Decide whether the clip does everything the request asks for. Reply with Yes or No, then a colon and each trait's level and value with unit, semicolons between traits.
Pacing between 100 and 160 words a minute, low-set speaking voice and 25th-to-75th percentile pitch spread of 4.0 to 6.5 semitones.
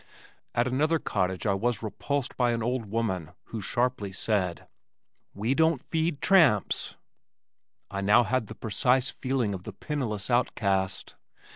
Yes: average, 140 wpm; low, 115 Hz; average, 4.5 semitones